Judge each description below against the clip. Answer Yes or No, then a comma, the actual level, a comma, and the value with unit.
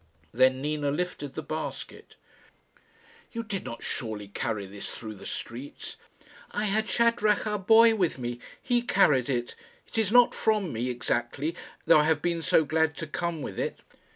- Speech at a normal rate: Yes, average, 170 wpm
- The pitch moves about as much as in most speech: No, wide, 8.9 semitones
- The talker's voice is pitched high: No, medium, 155 Hz